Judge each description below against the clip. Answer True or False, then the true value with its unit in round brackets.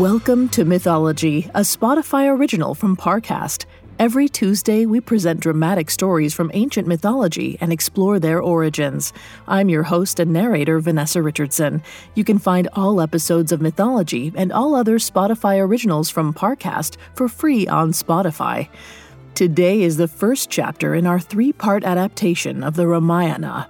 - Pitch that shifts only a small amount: False (4.4 semitones)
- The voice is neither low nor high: True (180 Hz)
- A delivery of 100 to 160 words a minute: True (150 wpm)